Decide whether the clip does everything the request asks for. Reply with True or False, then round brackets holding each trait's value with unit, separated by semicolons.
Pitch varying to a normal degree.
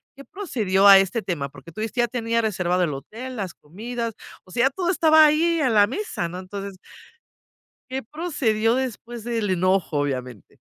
False (5.7 semitones)